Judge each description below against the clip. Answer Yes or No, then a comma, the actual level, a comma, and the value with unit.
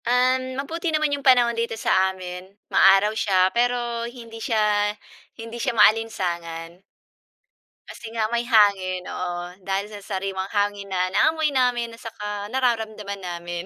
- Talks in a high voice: Yes, high, 215 Hz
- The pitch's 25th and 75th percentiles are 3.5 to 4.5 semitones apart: Yes, average, 3.9 semitones